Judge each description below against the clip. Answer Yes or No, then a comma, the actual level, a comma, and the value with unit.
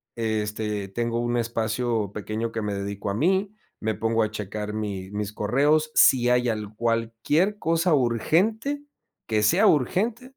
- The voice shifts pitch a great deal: Yes, wide, 5.8 semitones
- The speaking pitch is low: Yes, low, 115 Hz